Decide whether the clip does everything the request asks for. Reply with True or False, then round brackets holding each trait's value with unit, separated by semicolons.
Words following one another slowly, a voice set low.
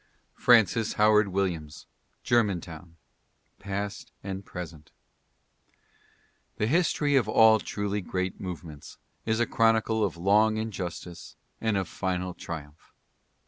True (105 wpm; 100 Hz)